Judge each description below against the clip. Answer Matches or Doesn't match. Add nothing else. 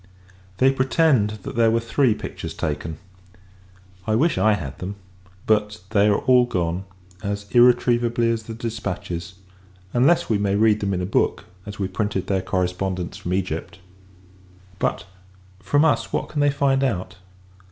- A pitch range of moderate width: Matches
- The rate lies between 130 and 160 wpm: Matches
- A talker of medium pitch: Doesn't match